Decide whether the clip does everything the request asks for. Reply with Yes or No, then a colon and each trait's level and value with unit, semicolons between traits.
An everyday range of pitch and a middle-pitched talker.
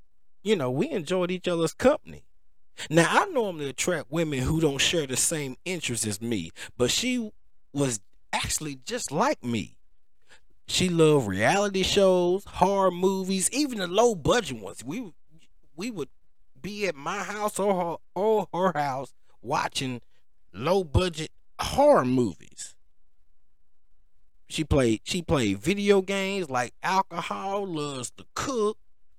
No: wide, 7.9 semitones; medium, 165 Hz